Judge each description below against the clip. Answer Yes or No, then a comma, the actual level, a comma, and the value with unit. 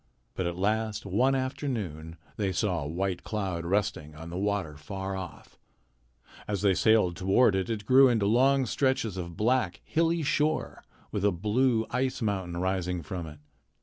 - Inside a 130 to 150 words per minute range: No, average, 165 wpm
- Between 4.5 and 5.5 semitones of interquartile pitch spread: Yes, average, 5.2 semitones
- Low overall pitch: Yes, low, 100 Hz